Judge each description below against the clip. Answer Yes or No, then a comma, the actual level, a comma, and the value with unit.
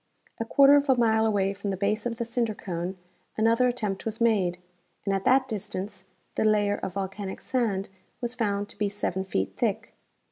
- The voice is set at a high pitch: Yes, high, 210 Hz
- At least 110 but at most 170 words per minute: No, average, 190 wpm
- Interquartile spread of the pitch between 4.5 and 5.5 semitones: No, average, 3.1 semitones